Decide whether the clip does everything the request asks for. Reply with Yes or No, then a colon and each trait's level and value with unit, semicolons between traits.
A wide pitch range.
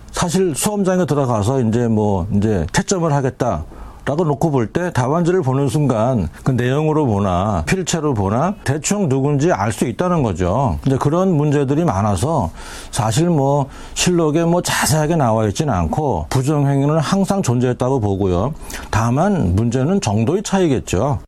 Yes: wide, 6.7 semitones